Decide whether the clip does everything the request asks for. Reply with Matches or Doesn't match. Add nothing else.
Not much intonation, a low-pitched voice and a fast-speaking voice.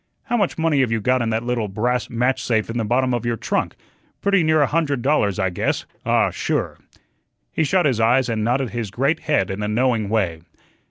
Doesn't match